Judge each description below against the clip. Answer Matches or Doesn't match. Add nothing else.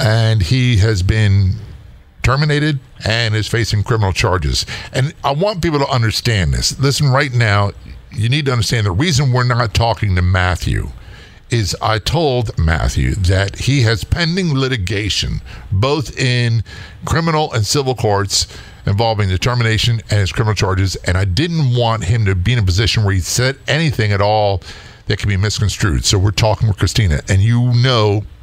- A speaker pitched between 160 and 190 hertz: Doesn't match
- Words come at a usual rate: Matches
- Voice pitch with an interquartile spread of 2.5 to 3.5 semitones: Doesn't match